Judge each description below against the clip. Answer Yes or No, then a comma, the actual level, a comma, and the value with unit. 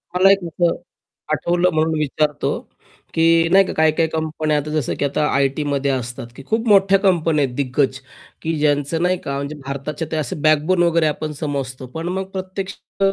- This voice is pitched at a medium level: Yes, medium, 155 Hz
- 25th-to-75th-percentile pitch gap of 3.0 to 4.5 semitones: Yes, average, 3.3 semitones